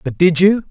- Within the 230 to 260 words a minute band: Yes, fast, 255 wpm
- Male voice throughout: Yes, male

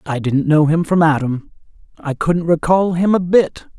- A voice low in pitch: No, medium, 165 Hz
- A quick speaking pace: No, average, 190 wpm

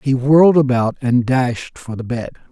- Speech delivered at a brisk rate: No, average, 190 wpm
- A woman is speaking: No, male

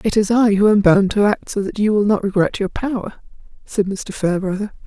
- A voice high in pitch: Yes, high, 205 Hz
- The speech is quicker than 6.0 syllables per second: No, 5.6 syllables/s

